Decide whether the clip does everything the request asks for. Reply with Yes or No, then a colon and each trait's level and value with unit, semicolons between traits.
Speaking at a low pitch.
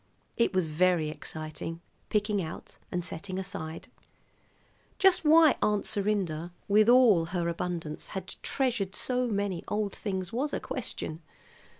No: high, 190 Hz